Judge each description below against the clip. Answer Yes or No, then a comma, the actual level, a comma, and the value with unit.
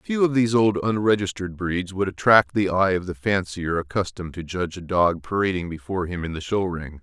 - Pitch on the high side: No, very low, 95 Hz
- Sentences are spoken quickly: Yes, fast, 215 wpm